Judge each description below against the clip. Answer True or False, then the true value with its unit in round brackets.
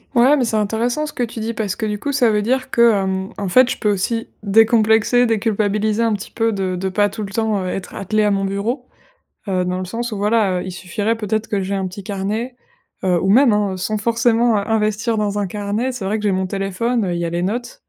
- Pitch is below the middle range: False (210 Hz)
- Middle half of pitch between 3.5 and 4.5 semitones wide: False (2.8 semitones)